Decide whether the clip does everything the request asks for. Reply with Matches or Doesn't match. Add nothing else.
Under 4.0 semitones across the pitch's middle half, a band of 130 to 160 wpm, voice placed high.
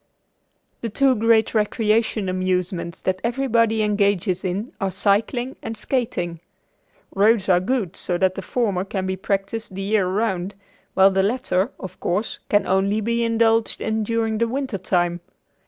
Matches